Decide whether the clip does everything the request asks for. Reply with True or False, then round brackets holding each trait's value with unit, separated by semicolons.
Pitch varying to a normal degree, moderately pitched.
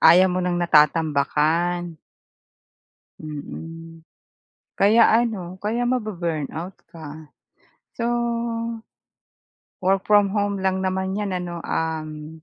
True (3.2 semitones; 175 Hz)